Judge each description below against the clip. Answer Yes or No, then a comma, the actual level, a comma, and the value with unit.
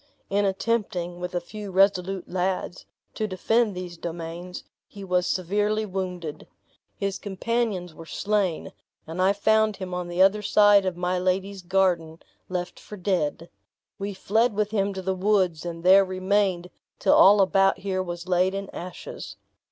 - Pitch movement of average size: No, narrow, 2.1 semitones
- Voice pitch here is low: No, high, 190 Hz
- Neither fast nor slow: Yes, average, 160 wpm